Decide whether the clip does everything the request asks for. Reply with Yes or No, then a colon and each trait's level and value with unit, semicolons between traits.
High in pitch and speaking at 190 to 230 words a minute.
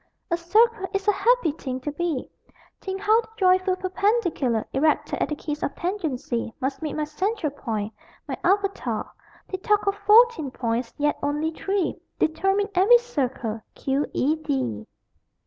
No: very high, 330 Hz; average, 155 wpm